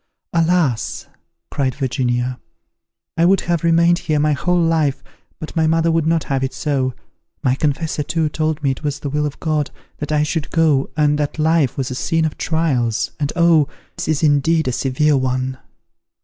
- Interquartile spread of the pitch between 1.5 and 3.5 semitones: Yes, average, 3.2 semitones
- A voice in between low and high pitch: Yes, medium, 150 Hz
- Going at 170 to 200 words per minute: Yes, average, 185 wpm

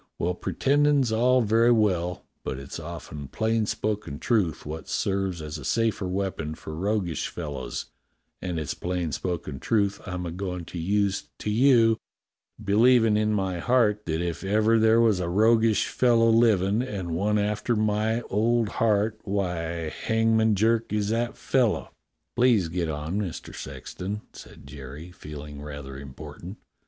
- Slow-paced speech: No, average, 150 wpm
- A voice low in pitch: Yes, low, 100 Hz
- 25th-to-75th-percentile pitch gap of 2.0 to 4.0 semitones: No, average, 4.9 semitones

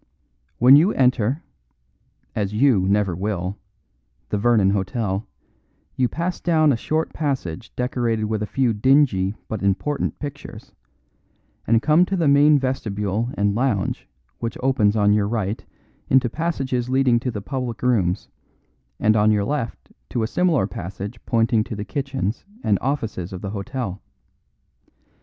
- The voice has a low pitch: Yes, low, 115 Hz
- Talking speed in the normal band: Yes, average, 145 wpm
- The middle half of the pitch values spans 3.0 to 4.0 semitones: No, average, 4.6 semitones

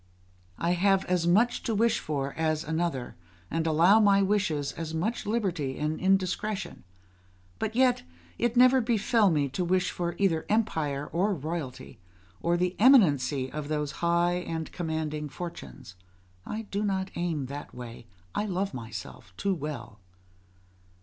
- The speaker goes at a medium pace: Yes, average, 145 wpm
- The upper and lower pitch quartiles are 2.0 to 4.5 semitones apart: No, average, 4.9 semitones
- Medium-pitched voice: Yes, medium, 170 Hz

